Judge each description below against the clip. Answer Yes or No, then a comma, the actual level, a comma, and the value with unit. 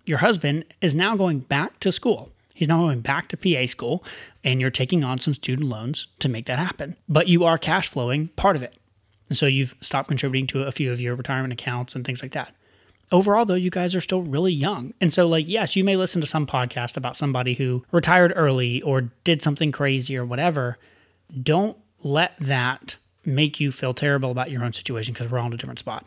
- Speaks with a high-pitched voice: No, medium, 140 Hz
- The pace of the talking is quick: Yes, fast, 225 wpm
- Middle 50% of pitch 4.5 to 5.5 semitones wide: Yes, average, 5.0 semitones